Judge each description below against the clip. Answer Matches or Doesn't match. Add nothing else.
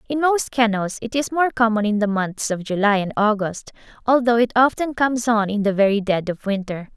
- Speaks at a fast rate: Matches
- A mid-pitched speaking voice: Doesn't match